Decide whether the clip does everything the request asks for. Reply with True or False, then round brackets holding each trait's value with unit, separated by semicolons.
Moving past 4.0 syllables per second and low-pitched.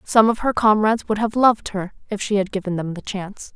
False (6.0 syllables/s; 205 Hz)